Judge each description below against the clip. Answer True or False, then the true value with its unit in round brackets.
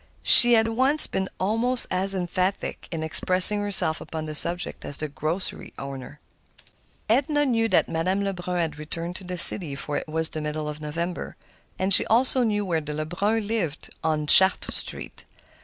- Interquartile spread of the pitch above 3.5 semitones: True (4.9 semitones)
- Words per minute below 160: False (175 wpm)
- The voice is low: False (180 Hz)